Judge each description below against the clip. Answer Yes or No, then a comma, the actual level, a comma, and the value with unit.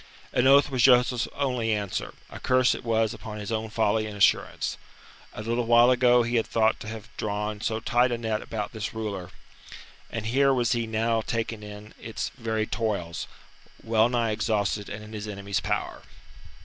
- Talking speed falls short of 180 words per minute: No, average, 185 wpm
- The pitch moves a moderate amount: No, narrow, 2.0 semitones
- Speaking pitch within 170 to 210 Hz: No, low, 110 Hz